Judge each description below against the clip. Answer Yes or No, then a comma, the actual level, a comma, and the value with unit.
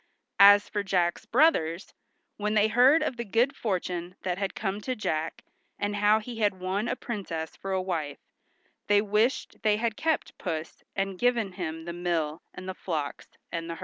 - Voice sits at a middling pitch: No, high, 200 Hz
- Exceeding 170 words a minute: Yes, average, 180 wpm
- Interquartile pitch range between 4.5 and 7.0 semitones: No, average, 3.8 semitones